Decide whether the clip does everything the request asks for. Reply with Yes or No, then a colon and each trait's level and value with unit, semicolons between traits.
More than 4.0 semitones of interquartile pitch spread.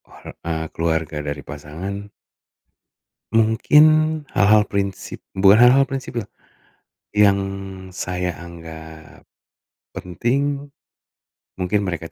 Yes: average, 4.9 semitones